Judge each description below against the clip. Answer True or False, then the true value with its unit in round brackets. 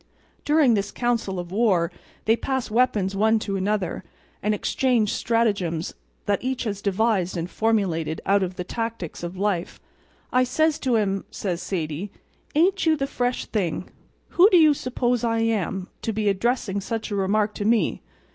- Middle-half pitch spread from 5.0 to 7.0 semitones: False (4.0 semitones)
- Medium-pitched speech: False (215 Hz)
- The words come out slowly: False (165 wpm)